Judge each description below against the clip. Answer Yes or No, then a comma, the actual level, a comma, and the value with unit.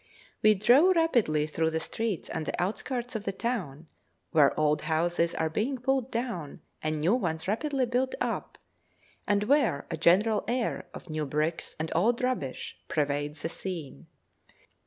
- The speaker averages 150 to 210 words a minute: Yes, average, 155 wpm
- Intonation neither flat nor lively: No, wide, 7.4 semitones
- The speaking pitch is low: No, medium, 185 Hz